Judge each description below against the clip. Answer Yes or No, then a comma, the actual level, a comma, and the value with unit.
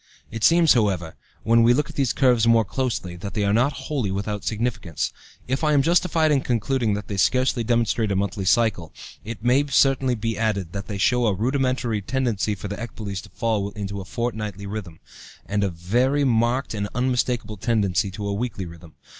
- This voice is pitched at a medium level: No, low, 115 Hz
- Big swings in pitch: No, average, 3.9 semitones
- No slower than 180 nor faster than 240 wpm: Yes, average, 195 wpm